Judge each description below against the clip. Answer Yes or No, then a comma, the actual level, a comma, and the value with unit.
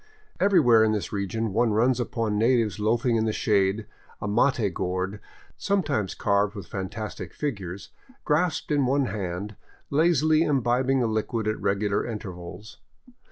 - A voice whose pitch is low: Yes, low, 110 Hz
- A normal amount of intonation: Yes, average, 4.2 semitones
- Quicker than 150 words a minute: No, average, 145 wpm